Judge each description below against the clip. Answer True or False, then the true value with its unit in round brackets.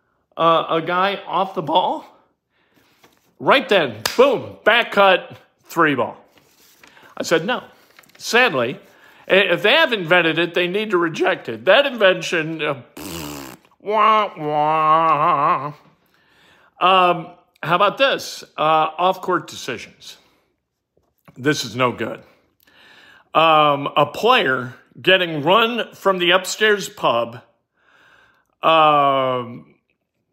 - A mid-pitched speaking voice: True (170 Hz)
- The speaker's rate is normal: False (105 wpm)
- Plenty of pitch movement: False (4.2 semitones)